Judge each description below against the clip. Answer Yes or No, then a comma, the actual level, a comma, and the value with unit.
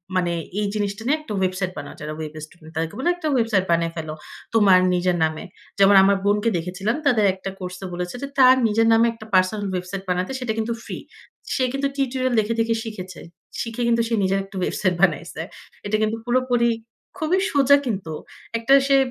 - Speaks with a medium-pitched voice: No, high, 205 Hz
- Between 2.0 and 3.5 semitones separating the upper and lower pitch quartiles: No, average, 4.5 semitones